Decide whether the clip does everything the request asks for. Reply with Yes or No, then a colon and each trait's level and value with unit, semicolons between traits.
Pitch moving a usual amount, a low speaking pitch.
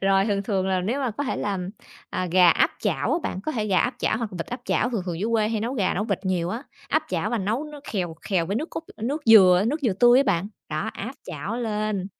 No: average, 4.3 semitones; high, 210 Hz